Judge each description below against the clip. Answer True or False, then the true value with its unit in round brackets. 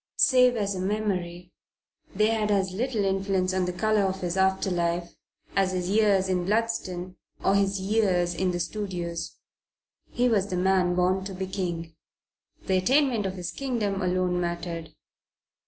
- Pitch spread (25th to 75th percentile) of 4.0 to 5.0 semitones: False (2.5 semitones)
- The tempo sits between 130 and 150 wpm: False (160 wpm)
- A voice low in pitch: False (190 Hz)